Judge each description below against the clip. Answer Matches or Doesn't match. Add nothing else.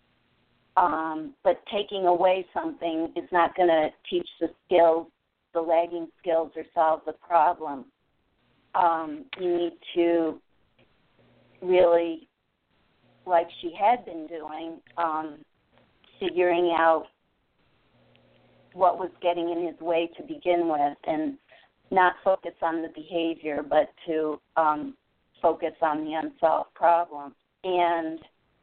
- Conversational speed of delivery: Doesn't match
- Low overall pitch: Doesn't match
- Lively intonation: Doesn't match